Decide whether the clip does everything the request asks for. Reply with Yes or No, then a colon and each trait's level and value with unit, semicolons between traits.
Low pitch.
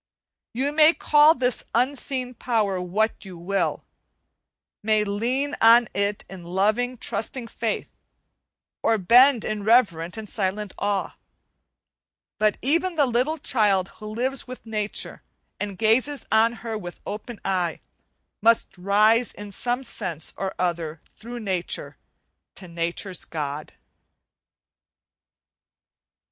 No: high, 215 Hz